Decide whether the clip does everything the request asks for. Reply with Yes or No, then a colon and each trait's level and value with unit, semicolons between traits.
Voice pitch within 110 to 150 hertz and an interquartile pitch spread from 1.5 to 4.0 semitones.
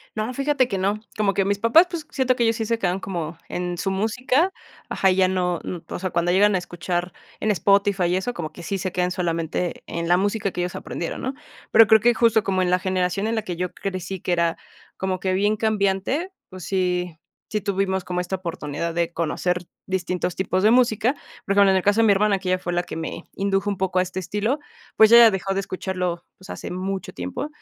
No: high, 190 Hz; average, 2.9 semitones